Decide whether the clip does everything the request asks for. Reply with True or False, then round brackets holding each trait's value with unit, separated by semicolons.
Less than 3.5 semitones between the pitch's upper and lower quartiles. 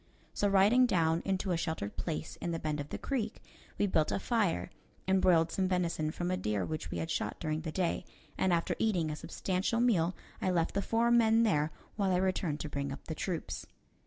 False (3.8 semitones)